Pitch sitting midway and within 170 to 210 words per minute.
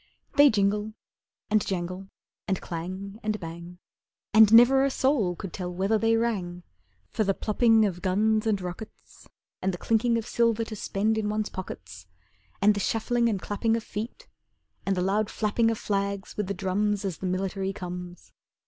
No: high, 205 Hz; average, 175 wpm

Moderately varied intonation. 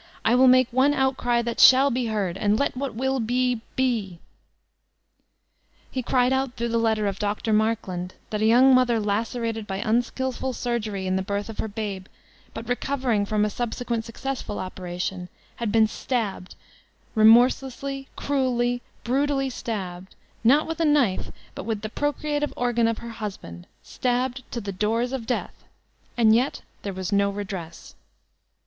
Yes: average, 3.7 semitones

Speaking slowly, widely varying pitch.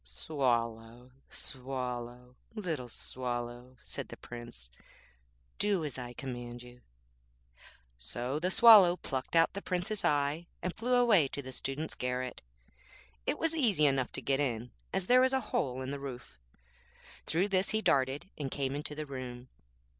No: average, 155 wpm; wide, 5.9 semitones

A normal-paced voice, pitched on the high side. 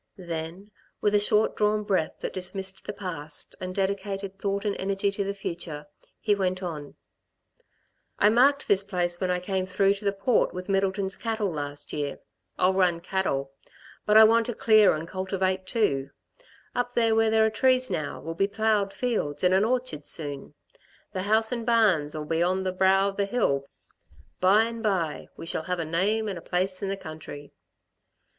Yes: average, 185 wpm; high, 195 Hz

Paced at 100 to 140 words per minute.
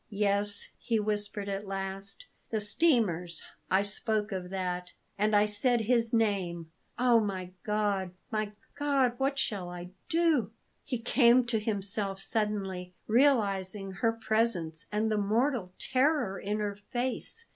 Yes: slow, 135 wpm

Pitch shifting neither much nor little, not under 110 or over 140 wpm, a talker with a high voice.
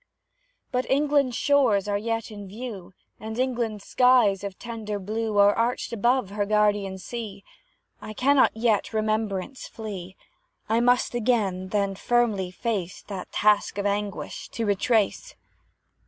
Yes: average, 3.1 semitones; slow, 135 wpm; high, 215 Hz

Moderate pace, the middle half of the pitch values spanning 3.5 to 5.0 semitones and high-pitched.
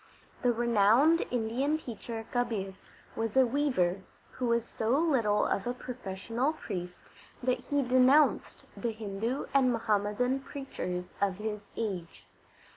No: slow, 125 wpm; average, 3.8 semitones; high, 235 Hz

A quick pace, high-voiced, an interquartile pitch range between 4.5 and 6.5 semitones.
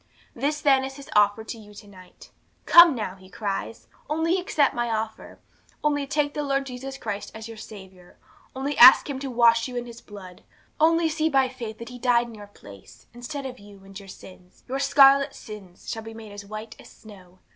Yes: fast, 210 wpm; high, 235 Hz; average, 5.0 semitones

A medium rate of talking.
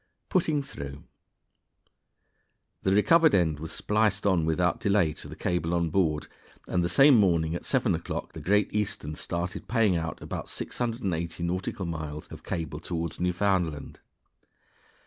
Yes: average, 145 wpm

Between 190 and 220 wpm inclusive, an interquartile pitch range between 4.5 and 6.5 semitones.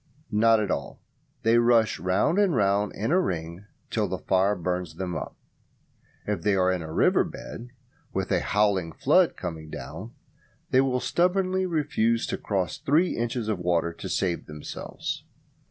No: average, 165 wpm; wide, 5.5 semitones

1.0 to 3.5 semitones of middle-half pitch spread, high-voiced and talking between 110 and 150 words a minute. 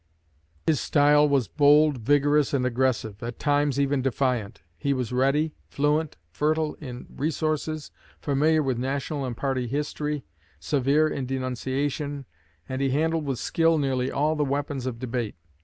No: narrow, 2.5 semitones; medium, 140 Hz; average, 145 wpm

